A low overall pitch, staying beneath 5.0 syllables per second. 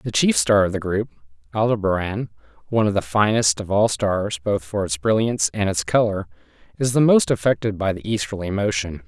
No: low, 100 Hz; 5.5 syllables/s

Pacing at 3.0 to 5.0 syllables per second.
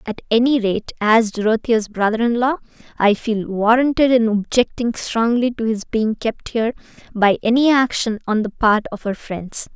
Yes: 4.7 syllables/s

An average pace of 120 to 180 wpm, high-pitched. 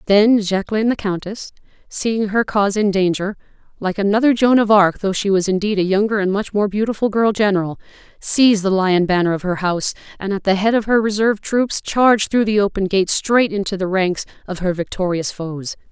No: average, 195 wpm; high, 200 Hz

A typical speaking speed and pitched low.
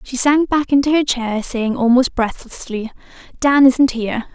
No: average, 165 wpm; very high, 255 Hz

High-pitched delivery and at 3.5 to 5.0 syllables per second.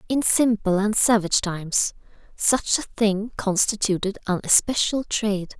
Yes: high, 210 Hz; 4.6 syllables/s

